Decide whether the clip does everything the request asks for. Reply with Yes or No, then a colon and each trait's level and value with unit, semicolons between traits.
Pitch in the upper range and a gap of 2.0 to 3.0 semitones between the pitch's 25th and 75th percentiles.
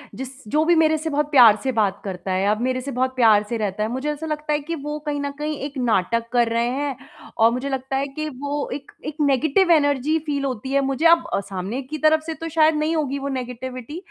No: very high, 275 Hz; average, 3.8 semitones